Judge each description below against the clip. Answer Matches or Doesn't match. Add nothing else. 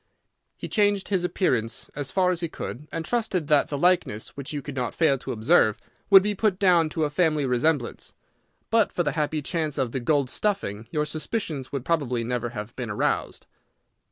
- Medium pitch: Matches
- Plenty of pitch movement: Matches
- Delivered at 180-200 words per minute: Matches